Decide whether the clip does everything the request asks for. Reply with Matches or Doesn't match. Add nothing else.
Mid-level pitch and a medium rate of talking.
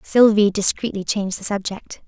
Doesn't match